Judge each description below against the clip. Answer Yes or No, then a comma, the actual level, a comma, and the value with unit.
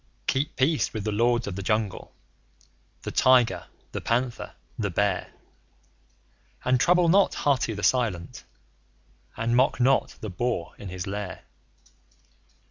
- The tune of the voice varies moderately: Yes, average, 4.1 semitones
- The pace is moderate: No, slow, 130 wpm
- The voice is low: Yes, low, 115 Hz